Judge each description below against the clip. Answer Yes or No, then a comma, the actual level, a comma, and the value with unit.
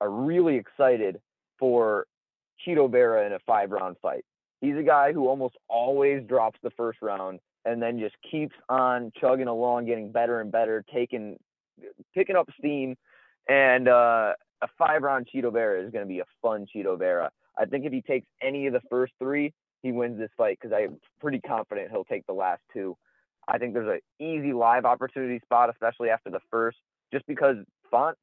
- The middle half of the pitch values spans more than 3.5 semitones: No, average, 3.2 semitones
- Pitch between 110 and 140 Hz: Yes, low, 125 Hz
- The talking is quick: No, average, 190 wpm